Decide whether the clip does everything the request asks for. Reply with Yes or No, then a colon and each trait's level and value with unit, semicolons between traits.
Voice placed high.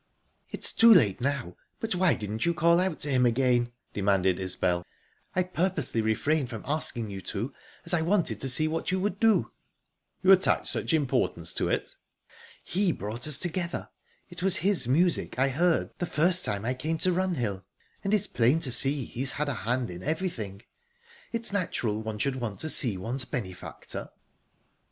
No: low, 135 Hz